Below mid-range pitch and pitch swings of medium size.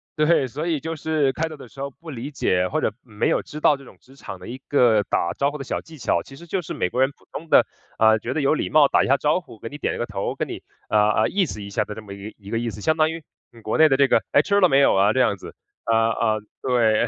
No: low, 130 Hz; wide, 5.8 semitones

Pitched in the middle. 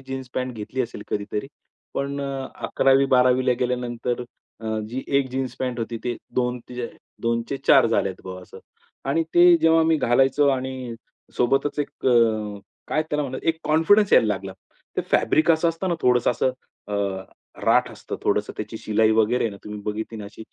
No: low, 125 Hz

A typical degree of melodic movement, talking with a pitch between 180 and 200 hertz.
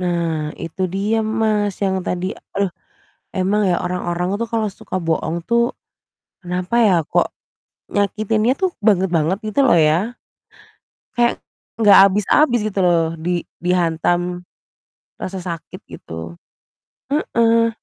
Yes: average, 3.8 semitones; high, 190 Hz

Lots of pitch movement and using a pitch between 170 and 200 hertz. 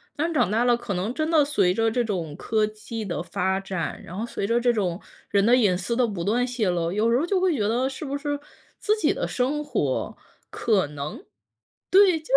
No: wide, 5.8 semitones; high, 225 Hz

